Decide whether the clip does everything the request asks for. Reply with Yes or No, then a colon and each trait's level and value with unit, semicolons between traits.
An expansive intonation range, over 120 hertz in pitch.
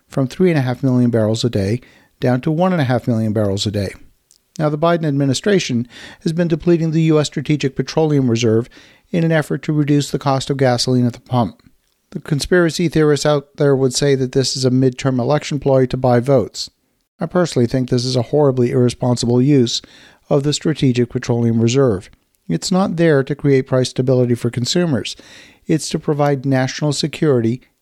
No: average, 3.5 semitones; low, 135 Hz